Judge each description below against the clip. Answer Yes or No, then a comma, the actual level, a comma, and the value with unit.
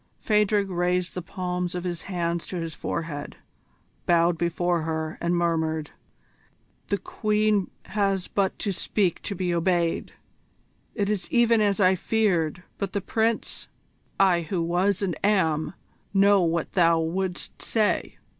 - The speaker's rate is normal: Yes, average, 145 wpm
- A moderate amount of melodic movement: Yes, average, 3.0 semitones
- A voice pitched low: No, medium, 180 Hz